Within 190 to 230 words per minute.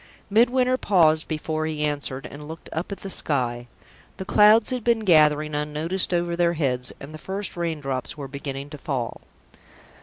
No: average, 175 wpm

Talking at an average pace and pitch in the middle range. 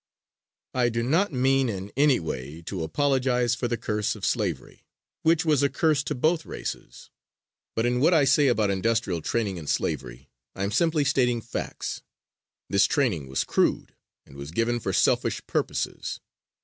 No: average, 165 wpm; low, 120 Hz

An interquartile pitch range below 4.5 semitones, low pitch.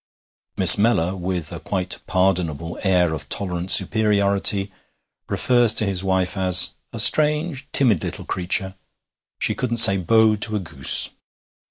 Yes: average, 3.5 semitones; very low, 95 Hz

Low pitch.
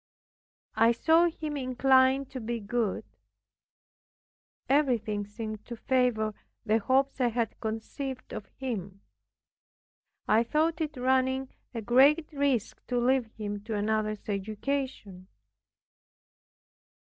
No: high, 245 Hz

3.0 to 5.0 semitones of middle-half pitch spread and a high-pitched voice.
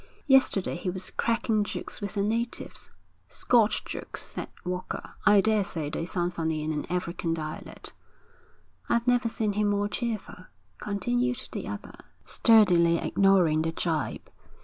Yes: average, 4.6 semitones; high, 195 Hz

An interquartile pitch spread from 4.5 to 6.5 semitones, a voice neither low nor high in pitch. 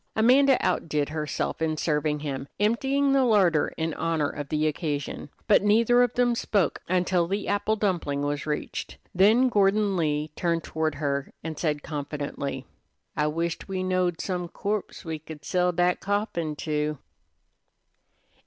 Yes: average, 5.2 semitones; medium, 170 Hz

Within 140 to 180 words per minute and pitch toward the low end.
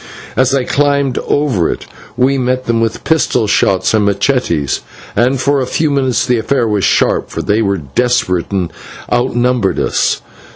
Yes: average, 165 wpm; low, 125 Hz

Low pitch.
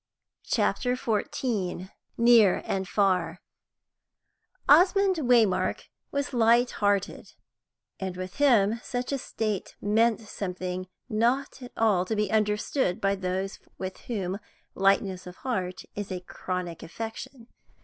No: high, 210 Hz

